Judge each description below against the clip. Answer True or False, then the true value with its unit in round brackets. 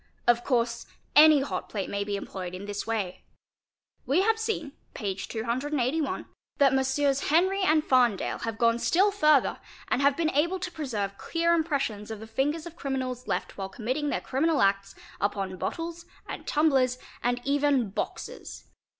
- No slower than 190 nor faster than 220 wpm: False (165 wpm)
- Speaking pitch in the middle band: False (265 Hz)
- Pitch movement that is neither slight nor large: False (5.8 semitones)